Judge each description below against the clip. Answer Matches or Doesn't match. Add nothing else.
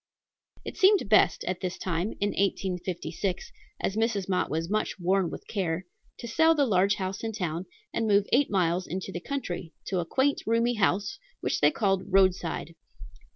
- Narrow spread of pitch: Doesn't match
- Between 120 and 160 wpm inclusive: Doesn't match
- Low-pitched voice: Doesn't match